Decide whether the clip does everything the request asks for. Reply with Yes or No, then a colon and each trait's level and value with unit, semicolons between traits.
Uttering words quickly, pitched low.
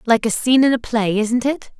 No: fast, 270 wpm; high, 235 Hz